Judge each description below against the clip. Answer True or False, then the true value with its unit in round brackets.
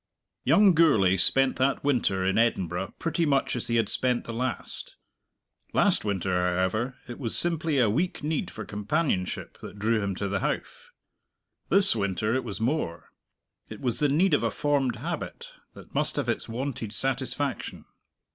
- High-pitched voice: False (120 Hz)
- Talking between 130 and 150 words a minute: False (165 wpm)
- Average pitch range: False (6.0 semitones)